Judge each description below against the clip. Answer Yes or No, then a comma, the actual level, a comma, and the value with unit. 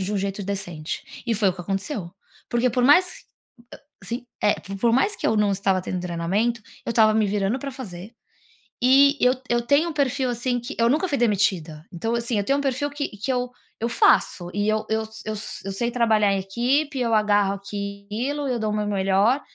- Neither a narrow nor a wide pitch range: Yes, average, 4.1 semitones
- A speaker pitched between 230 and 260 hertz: No, high, 220 Hz